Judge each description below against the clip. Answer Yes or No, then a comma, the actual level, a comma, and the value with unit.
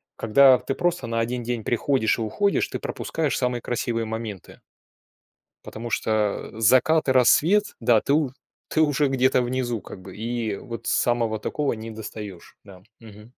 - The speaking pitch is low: Yes, low, 120 Hz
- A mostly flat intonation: No, average, 3.1 semitones